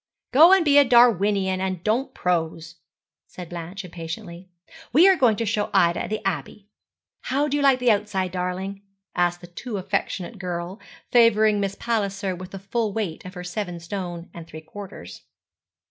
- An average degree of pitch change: Yes, average, 3.8 semitones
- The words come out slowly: No, average, 170 wpm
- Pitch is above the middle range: Yes, high, 195 Hz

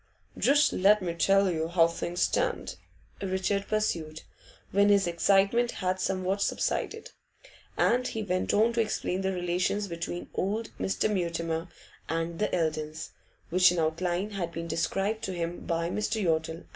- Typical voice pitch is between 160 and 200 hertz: Yes, medium, 185 Hz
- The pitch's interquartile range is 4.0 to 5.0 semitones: No, average, 3.2 semitones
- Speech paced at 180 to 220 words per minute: No, average, 150 wpm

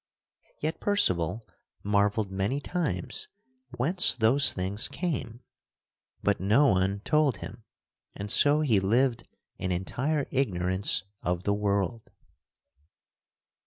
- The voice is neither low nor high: No, low, 105 Hz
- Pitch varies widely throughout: Yes, wide, 6.3 semitones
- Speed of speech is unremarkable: No, slow, 105 wpm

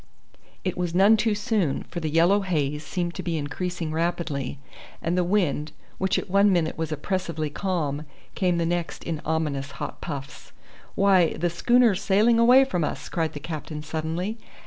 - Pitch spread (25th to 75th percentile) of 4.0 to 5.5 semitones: No, average, 3.6 semitones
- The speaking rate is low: No, average, 170 wpm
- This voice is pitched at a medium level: Yes, medium, 170 Hz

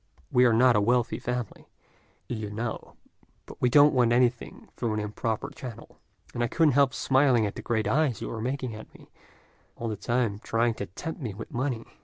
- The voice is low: Yes, low, 120 Hz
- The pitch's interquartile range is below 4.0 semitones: Yes, narrow, 2.5 semitones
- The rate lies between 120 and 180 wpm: No, average, 200 wpm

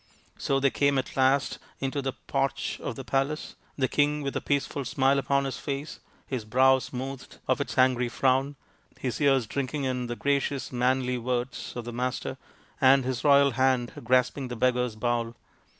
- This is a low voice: Yes, low, 130 Hz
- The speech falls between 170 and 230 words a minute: Yes, average, 175 wpm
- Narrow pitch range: Yes, narrow, 1.8 semitones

